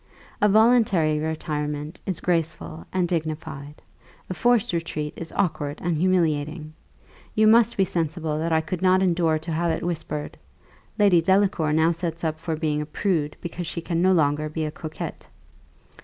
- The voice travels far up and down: No, average, 2.9 semitones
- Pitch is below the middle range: No, medium, 165 Hz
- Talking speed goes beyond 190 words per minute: No, average, 165 wpm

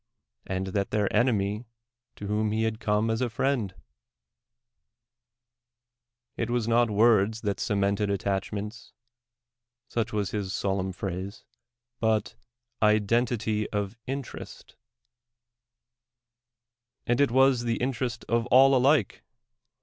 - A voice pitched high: No, low, 110 Hz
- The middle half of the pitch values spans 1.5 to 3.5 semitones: Yes, average, 2.9 semitones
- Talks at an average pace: No, slow, 110 wpm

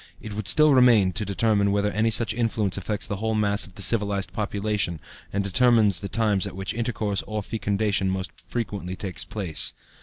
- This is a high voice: No, low, 105 Hz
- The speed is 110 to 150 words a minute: No, average, 185 wpm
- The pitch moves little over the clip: Yes, narrow, 2.0 semitones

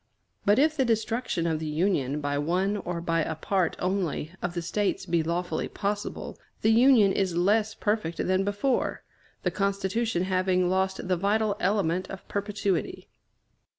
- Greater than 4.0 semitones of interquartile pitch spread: No, average, 3.3 semitones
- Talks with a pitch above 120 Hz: Yes, high, 190 Hz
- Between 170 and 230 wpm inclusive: No, average, 155 wpm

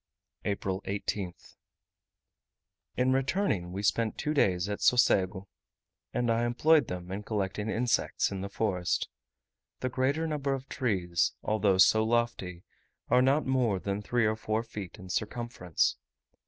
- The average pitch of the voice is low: Yes, low, 110 Hz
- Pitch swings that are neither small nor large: Yes, average, 4.6 semitones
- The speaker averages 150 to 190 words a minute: No, average, 140 wpm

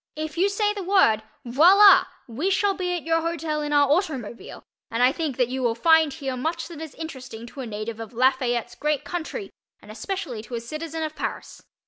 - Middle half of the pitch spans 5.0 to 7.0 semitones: Yes, wide, 5.4 semitones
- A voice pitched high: Yes, very high, 300 Hz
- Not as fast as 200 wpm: No, fast, 205 wpm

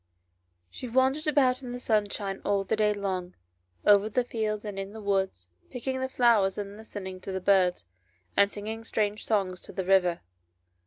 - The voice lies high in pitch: Yes, high, 205 Hz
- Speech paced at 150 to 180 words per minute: Yes, average, 175 wpm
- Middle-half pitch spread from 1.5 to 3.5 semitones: Yes, average, 2.8 semitones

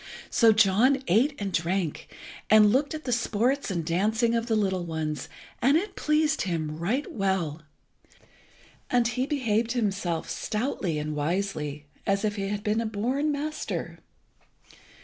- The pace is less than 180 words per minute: Yes, average, 150 wpm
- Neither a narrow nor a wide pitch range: No, wide, 6.0 semitones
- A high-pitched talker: Yes, high, 210 Hz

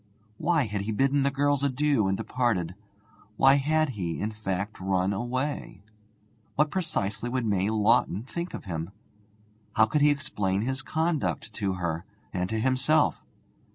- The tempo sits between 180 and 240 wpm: No, average, 155 wpm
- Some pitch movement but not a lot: No, wide, 6.4 semitones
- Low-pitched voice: Yes, low, 115 Hz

